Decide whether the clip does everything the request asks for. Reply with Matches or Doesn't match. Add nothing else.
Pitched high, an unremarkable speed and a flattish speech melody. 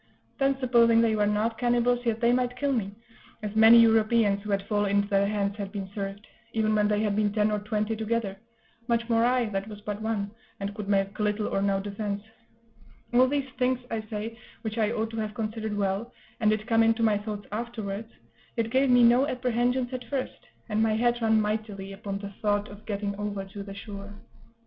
Doesn't match